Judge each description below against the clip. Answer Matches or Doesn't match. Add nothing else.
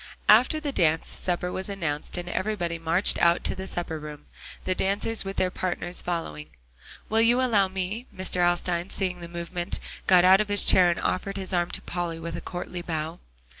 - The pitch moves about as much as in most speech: Doesn't match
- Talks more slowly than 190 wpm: Doesn't match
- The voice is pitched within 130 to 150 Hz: Doesn't match